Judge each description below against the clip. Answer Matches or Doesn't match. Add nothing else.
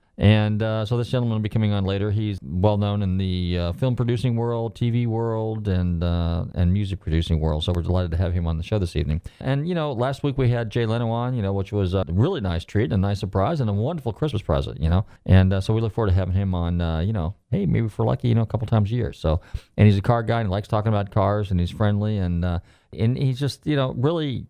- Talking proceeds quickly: Matches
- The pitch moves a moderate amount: Matches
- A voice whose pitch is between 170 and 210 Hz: Doesn't match